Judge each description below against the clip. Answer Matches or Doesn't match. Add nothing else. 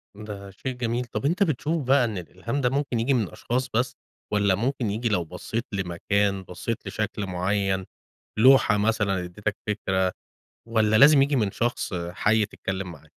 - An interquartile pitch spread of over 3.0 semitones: Matches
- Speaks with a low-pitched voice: Matches